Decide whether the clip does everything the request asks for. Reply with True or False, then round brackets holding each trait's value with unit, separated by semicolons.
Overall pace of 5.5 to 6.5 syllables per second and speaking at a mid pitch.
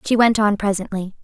False (5.9 syllables/s; 205 Hz)